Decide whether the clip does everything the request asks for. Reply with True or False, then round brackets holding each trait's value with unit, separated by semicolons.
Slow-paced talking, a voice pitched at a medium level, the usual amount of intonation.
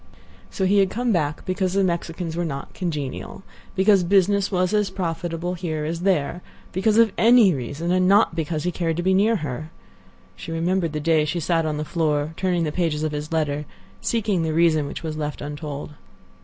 False (195 wpm; 170 Hz; 3.6 semitones)